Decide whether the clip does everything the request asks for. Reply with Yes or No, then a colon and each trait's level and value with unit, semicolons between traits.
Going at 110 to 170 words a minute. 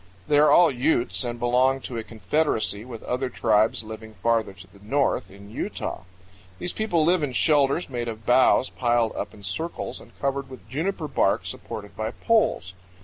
No: average, 180 wpm